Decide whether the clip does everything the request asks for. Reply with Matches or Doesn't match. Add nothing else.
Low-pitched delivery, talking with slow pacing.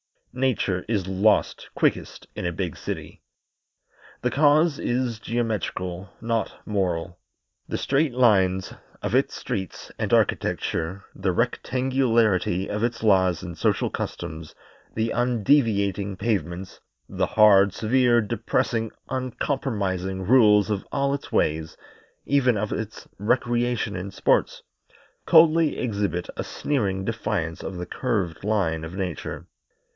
Matches